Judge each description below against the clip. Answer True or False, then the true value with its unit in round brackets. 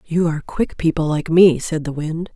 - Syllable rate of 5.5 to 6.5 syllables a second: False (5.0 syllables/s)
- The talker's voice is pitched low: False (160 Hz)